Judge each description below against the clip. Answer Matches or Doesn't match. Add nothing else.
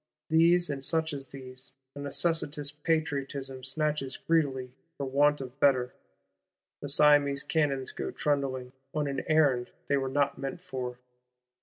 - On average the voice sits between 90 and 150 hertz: Matches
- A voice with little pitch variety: Matches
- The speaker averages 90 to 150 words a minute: Matches